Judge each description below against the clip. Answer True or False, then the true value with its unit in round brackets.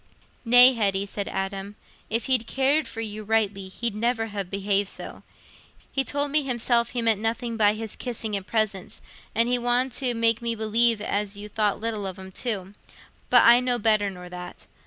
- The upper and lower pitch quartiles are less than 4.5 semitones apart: True (2.9 semitones)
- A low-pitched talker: False (220 Hz)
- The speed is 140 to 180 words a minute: False (190 wpm)